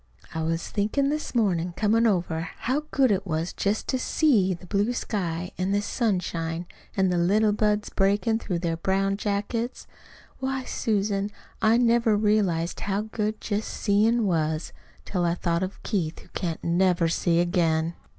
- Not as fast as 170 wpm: Yes, average, 160 wpm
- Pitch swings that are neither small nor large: Yes, average, 4.0 semitones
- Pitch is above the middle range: Yes, high, 195 Hz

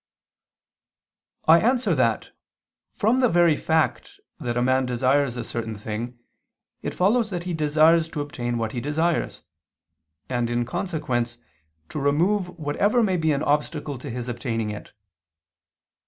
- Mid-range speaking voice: Yes, medium, 145 Hz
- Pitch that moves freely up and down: Yes, wide, 6.0 semitones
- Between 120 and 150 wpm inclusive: Yes, average, 140 wpm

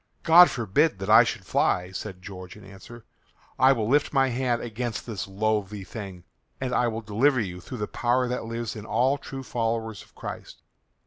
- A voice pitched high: No, low, 115 Hz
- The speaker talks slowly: No, average, 190 wpm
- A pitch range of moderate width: Yes, average, 3.7 semitones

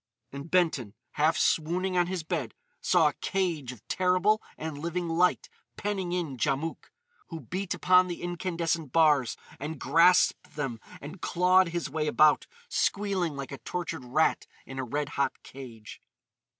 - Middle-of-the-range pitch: Yes, medium, 165 Hz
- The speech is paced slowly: No, average, 150 wpm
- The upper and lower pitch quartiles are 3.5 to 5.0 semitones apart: Yes, average, 4.0 semitones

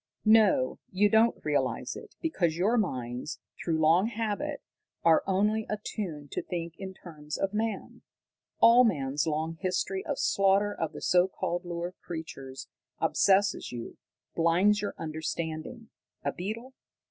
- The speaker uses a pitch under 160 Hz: No, medium, 185 Hz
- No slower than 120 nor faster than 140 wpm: Yes, slow, 135 wpm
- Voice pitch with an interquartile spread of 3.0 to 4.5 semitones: No, average, 4.9 semitones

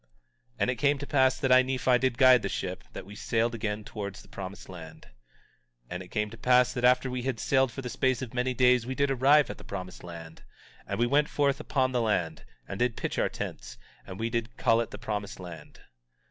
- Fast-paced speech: Yes, fast, 240 wpm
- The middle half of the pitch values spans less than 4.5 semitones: Yes, average, 4.1 semitones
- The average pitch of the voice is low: Yes, low, 120 Hz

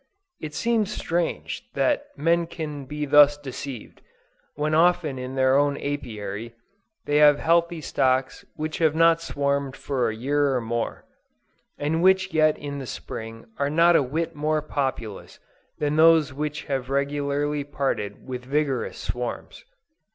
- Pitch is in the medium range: Yes, medium, 145 Hz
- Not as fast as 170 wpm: Yes, average, 145 wpm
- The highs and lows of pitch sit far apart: No, average, 3.0 semitones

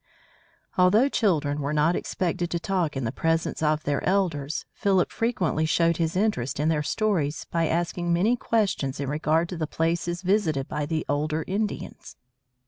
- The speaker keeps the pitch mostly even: No, average, 3.6 semitones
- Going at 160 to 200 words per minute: Yes, average, 165 wpm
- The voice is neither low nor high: Yes, medium, 165 Hz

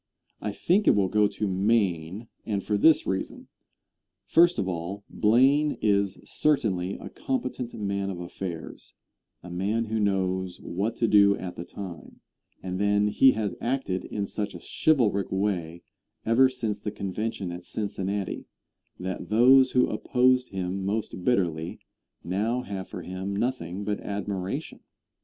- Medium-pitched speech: No, low, 100 Hz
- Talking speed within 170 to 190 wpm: No, average, 145 wpm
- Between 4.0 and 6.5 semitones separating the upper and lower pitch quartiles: No, average, 3.4 semitones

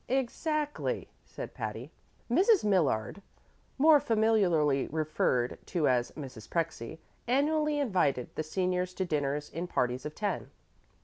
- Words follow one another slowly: Yes, slow, 120 wpm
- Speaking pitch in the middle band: Yes, medium, 180 Hz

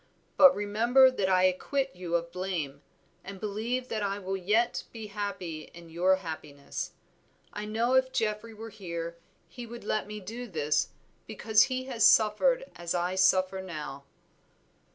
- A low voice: No, high, 200 Hz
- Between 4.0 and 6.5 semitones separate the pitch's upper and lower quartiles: Yes, average, 4.4 semitones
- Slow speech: No, average, 155 wpm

